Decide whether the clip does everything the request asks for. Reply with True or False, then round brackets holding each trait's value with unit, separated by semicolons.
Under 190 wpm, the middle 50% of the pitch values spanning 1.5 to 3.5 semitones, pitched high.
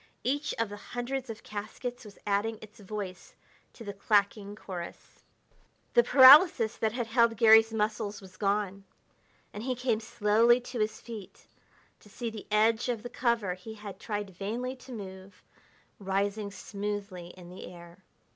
True (155 wpm; 2.7 semitones; 215 Hz)